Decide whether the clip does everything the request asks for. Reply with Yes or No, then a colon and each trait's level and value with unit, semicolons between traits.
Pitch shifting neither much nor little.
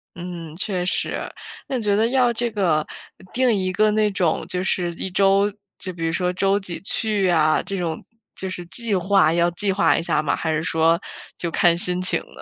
Yes: average, 3.1 semitones